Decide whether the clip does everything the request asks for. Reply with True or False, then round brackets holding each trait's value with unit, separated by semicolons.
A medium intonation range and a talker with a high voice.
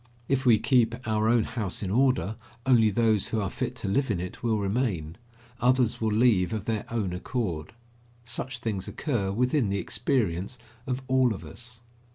False (4.0 semitones; 110 Hz)